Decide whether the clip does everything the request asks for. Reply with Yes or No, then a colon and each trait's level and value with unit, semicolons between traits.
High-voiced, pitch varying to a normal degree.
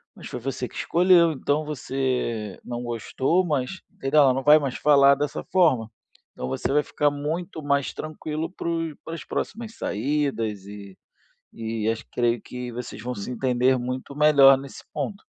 No: low, 135 Hz; average, 3.9 semitones